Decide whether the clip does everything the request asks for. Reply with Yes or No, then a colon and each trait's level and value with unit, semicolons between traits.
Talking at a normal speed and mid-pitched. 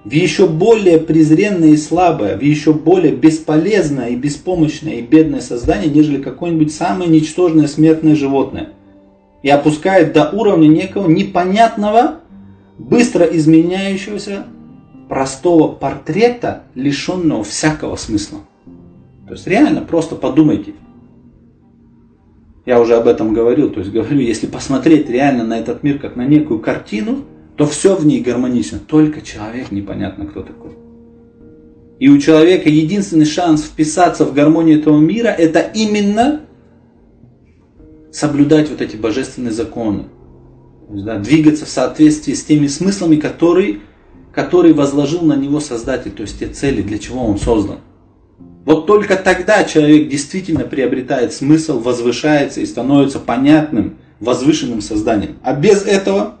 Yes: average, 130 wpm; medium, 155 Hz